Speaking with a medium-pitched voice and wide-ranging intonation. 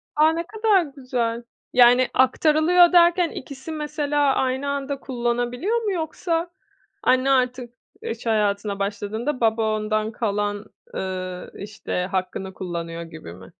No: high, 245 Hz; wide, 6.3 semitones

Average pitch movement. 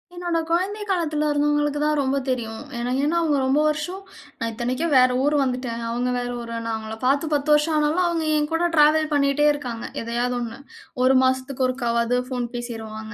Yes: average, 3.9 semitones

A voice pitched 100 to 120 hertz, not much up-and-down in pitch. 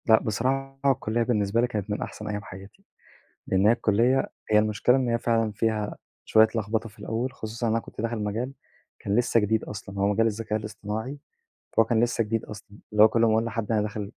Yes: low, 110 Hz; narrow, 1.8 semitones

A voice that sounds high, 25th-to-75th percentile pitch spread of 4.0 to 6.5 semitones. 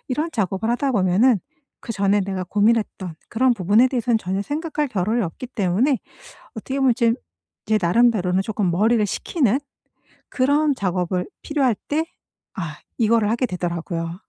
Yes: high, 220 Hz; average, 5.3 semitones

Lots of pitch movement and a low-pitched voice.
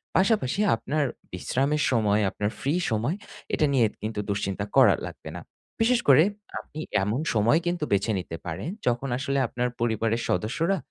Yes: wide, 6.2 semitones; low, 120 Hz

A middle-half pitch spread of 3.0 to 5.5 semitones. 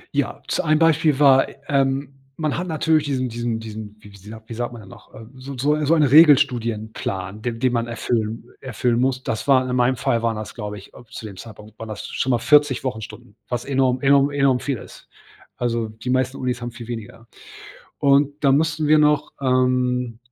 Yes: average, 3.6 semitones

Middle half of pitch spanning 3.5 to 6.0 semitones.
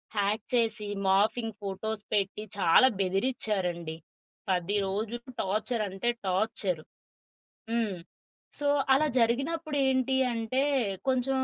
Yes: average, 4.0 semitones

